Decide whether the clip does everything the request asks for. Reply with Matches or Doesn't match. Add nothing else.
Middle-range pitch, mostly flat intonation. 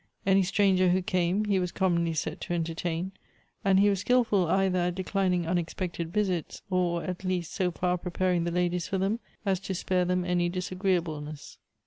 Matches